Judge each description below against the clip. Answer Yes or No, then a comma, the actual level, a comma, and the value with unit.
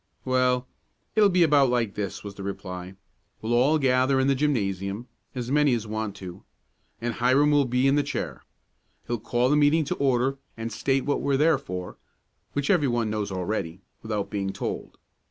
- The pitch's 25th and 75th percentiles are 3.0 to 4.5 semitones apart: No, average, 4.9 semitones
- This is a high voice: No, low, 125 Hz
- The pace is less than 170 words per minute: No, average, 185 wpm